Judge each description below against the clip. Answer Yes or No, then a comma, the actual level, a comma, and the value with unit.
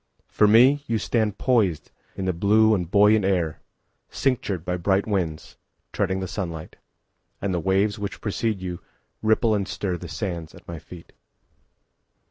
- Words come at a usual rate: No, slow, 120 wpm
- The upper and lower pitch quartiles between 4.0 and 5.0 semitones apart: No, average, 3.3 semitones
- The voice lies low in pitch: Yes, low, 100 Hz